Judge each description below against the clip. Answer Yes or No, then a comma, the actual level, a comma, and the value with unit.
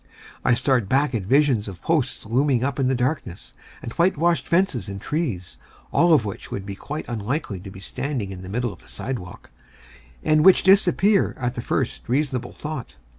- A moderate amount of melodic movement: No, wide, 6.4 semitones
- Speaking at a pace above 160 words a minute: Yes, average, 185 wpm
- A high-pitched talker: No, low, 130 Hz